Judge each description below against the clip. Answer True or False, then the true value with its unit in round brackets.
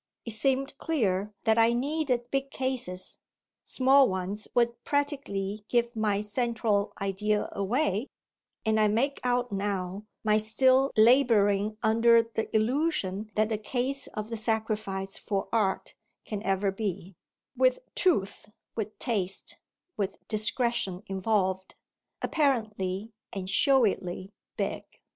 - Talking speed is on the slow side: True (120 wpm)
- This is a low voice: False (220 Hz)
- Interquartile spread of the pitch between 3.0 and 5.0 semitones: True (3.8 semitones)